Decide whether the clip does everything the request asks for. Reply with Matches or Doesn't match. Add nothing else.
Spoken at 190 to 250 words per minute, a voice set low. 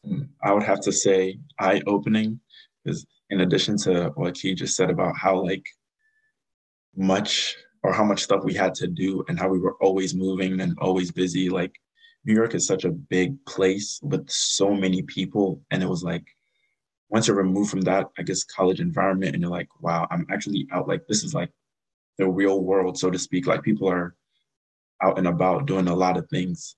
Matches